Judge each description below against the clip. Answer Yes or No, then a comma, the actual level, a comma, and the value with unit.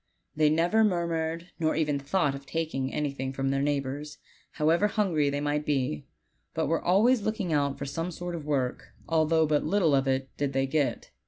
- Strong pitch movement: No, average, 3.2 semitones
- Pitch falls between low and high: Yes, medium, 150 Hz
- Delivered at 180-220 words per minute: Yes, average, 190 wpm